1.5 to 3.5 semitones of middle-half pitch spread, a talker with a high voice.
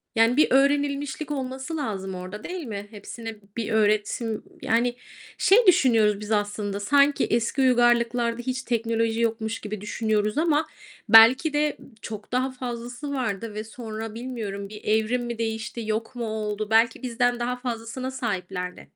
Yes: average, 3.0 semitones; high, 230 Hz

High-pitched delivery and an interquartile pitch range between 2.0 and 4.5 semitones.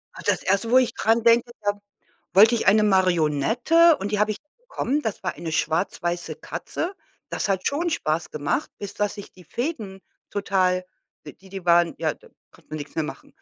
No: high, 200 Hz; average, 4.9 semitones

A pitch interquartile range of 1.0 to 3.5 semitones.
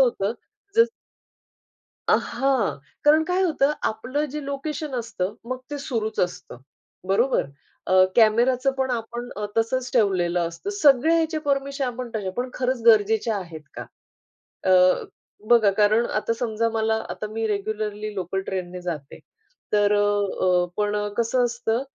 No: average, 4.2 semitones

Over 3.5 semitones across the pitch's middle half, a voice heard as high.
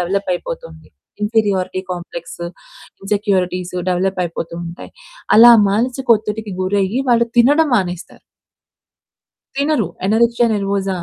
Yes: average, 4.0 semitones; high, 200 Hz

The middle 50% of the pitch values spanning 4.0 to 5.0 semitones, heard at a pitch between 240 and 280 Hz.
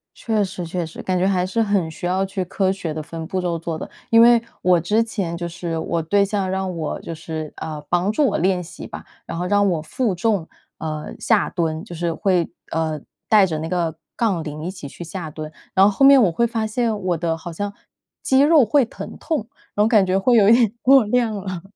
No: average, 4.3 semitones; medium, 185 Hz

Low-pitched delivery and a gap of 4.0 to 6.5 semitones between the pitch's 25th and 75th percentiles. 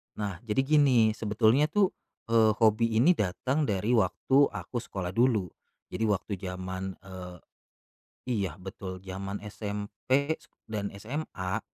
Yes: low, 105 Hz; average, 4.6 semitones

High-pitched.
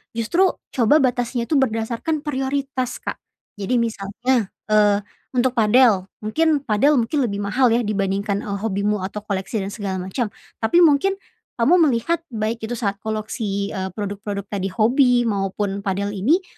Yes: high, 220 Hz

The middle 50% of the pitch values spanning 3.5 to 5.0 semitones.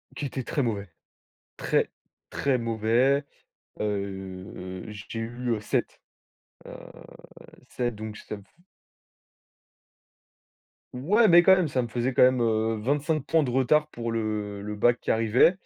Yes: average, 4.0 semitones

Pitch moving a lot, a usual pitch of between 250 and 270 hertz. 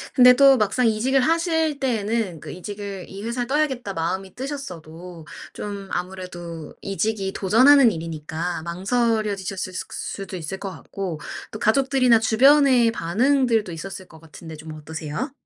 No: wide, 6.2 semitones; high, 200 Hz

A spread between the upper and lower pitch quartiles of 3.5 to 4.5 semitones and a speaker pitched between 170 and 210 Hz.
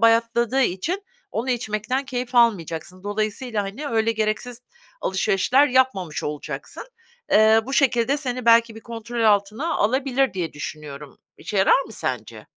No: average, 3.8 semitones; high, 230 Hz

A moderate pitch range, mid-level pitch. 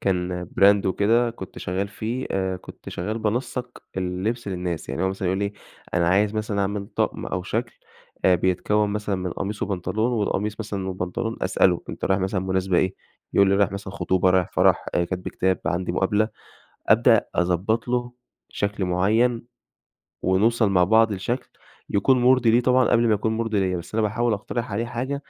No: average, 3.3 semitones; low, 100 Hz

